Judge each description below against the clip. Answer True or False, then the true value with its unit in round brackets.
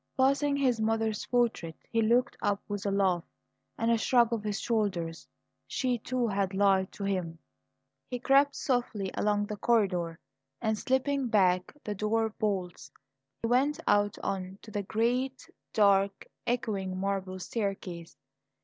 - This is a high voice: True (210 Hz)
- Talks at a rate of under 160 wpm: True (140 wpm)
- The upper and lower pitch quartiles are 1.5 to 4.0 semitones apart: True (3.7 semitones)